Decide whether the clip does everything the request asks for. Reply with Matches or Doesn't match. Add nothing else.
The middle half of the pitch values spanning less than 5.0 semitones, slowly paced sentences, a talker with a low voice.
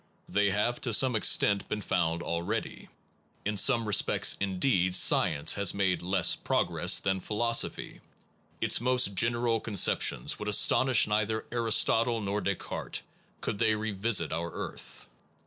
Matches